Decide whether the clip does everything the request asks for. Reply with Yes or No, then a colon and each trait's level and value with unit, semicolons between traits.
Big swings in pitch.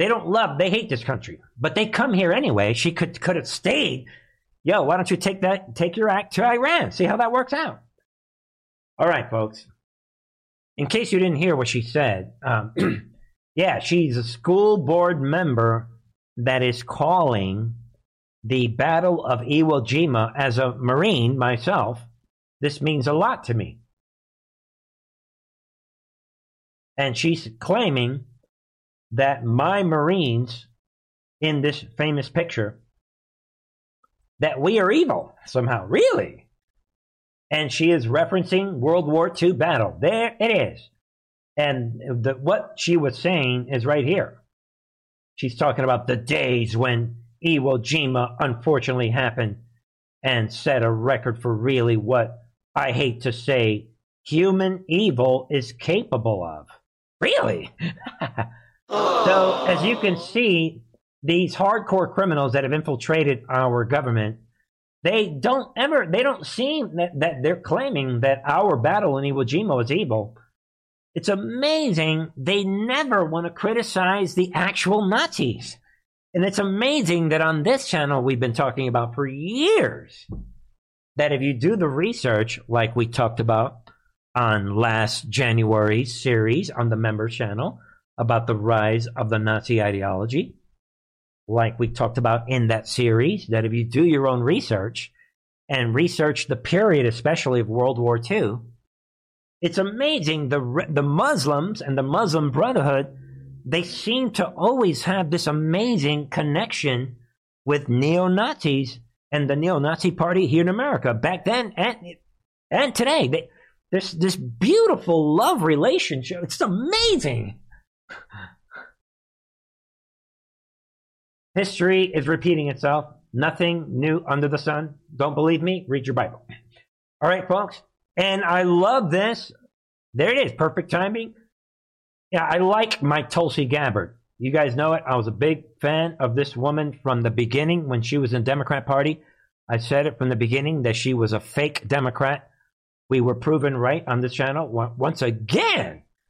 Yes: wide, 6.4 semitones